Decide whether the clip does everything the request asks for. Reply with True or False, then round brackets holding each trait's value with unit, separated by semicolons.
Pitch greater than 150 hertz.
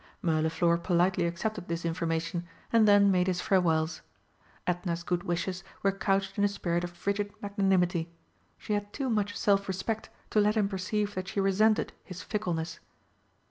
True (190 Hz)